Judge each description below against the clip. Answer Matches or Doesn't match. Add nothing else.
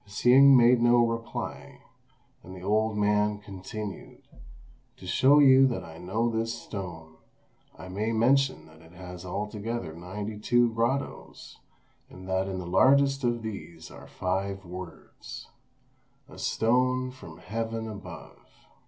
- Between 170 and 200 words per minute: Doesn't match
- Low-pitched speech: Matches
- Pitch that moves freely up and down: Doesn't match